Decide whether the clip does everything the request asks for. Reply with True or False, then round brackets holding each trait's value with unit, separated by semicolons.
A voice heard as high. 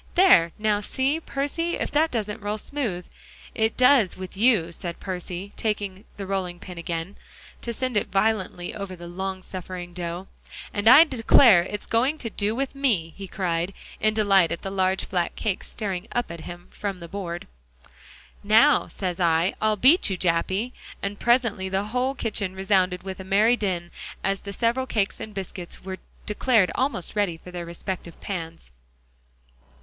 True (195 Hz)